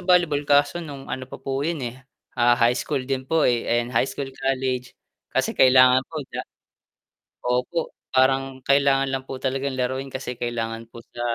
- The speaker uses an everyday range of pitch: No, narrow, 1.8 semitones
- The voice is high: No, low, 130 Hz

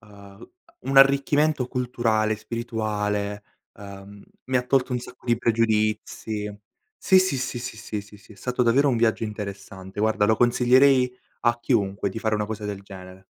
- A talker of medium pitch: No, low, 110 Hz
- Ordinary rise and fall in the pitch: Yes, average, 3.2 semitones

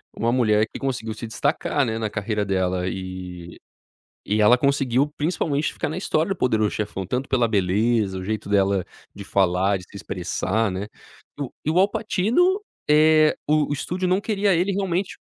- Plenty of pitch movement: Yes, wide, 7.6 semitones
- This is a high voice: No, low, 115 Hz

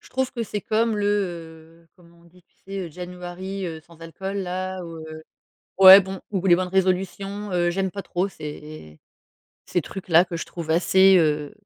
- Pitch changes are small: Yes, narrow, 2.3 semitones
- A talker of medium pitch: Yes, medium, 180 Hz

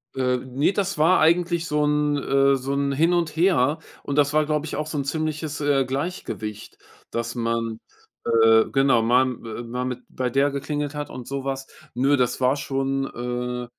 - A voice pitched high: No, low, 135 Hz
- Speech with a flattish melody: No, average, 3.1 semitones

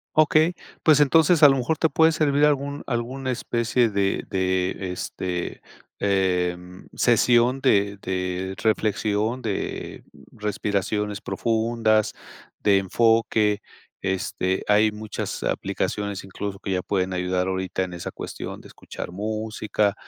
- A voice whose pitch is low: Yes, low, 105 Hz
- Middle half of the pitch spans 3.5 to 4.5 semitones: Yes, average, 4.1 semitones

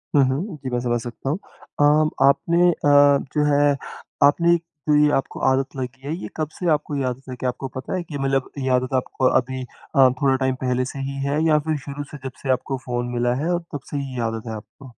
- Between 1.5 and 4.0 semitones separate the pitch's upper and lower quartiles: Yes, narrow, 2.5 semitones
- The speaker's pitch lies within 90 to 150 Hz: Yes, low, 135 Hz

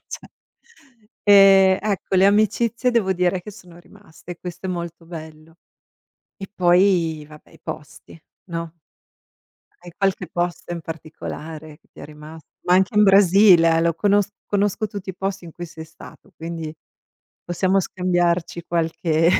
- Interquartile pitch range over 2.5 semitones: Yes, average, 2.9 semitones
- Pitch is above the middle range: No, medium, 175 Hz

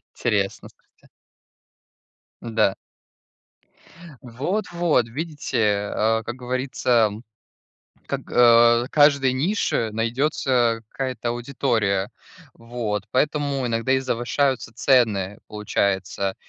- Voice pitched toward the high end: No, low, 120 Hz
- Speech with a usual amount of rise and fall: Yes, average, 3.0 semitones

